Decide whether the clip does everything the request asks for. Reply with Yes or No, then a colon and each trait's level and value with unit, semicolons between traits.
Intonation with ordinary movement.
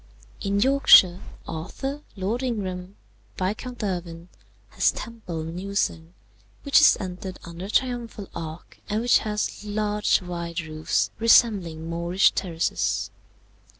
Yes: average, 4.4 semitones